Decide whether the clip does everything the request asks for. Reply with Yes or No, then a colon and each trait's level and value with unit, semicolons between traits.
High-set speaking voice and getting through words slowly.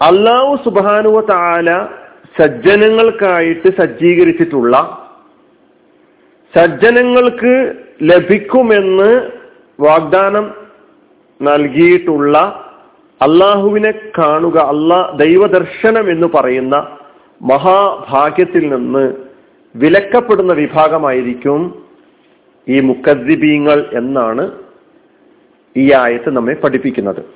Yes: high, 200 Hz; slow, 55 wpm